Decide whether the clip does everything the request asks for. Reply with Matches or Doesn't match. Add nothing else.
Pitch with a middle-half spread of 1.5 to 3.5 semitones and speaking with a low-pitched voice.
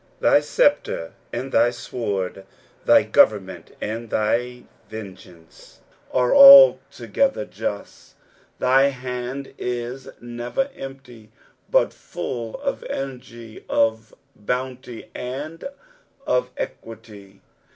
Matches